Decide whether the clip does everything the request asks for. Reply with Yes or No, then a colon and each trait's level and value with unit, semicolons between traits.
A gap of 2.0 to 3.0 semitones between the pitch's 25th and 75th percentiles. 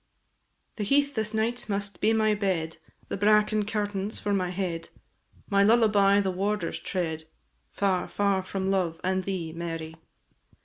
Yes: narrow, 2.5 semitones